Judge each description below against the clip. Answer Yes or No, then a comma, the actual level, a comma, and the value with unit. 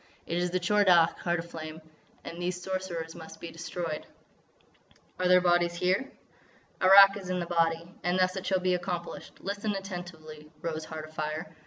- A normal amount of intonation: No, narrow, 2.0 semitones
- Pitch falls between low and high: Yes, medium, 175 Hz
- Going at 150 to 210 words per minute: Yes, average, 175 wpm